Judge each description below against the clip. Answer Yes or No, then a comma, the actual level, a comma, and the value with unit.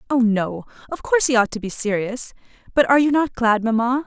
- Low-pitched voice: No, high, 240 Hz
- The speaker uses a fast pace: Yes, fast, 220 wpm